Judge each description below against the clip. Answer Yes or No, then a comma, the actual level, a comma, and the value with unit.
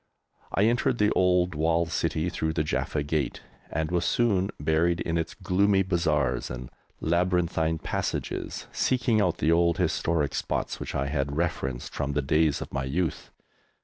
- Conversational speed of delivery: Yes, average, 160 wpm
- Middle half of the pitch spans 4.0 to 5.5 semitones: No, average, 3.3 semitones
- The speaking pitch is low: Yes, very low, 80 Hz